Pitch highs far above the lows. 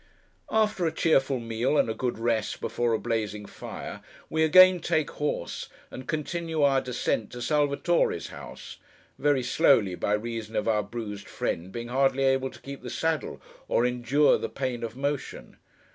No: average, 4.4 semitones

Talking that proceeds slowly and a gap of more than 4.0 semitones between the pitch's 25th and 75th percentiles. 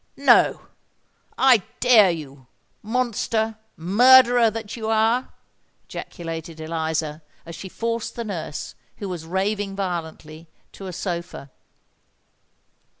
Yes: slow, 95 wpm; wide, 5.5 semitones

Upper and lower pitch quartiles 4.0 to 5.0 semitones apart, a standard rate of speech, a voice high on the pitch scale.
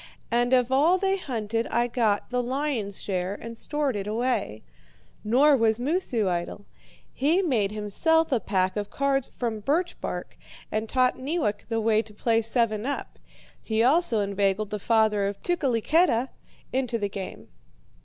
Yes: average, 4.5 semitones; average, 155 wpm; high, 230 Hz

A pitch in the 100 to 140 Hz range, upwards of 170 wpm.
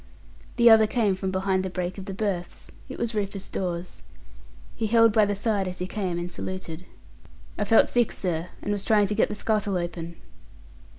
No: high, 195 Hz; average, 195 wpm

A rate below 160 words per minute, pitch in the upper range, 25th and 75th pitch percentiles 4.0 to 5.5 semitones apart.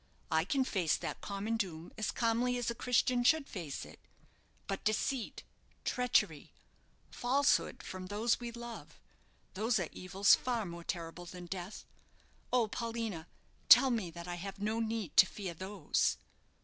Yes: average, 150 wpm; high, 210 Hz; average, 4.7 semitones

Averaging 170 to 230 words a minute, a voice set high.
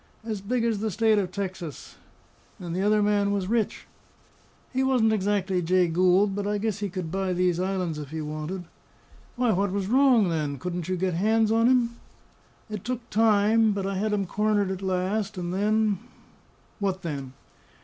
Yes: average, 185 wpm; high, 200 Hz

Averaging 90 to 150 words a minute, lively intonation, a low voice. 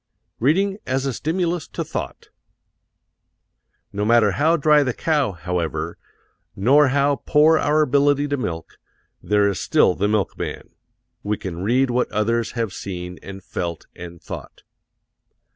Yes: average, 140 wpm; wide, 7.0 semitones; low, 120 Hz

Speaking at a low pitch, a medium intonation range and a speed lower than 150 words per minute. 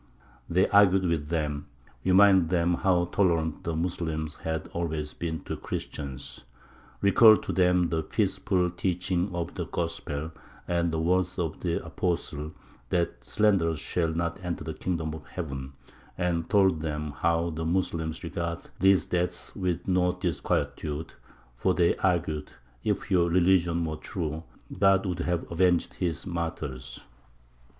No: very low, 85 Hz; narrow, 2.2 semitones; average, 140 wpm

